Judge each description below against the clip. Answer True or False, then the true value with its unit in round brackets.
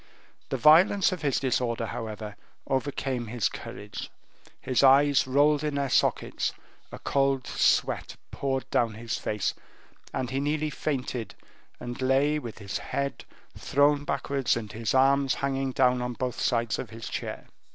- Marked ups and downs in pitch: False (3.0 semitones)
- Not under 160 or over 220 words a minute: False (150 wpm)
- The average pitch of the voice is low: True (130 Hz)